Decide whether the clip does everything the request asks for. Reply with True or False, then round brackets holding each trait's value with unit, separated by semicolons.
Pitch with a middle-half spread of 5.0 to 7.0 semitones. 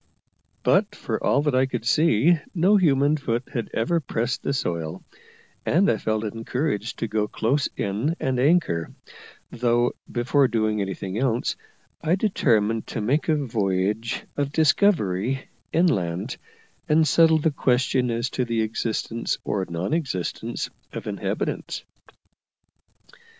True (5.4 semitones)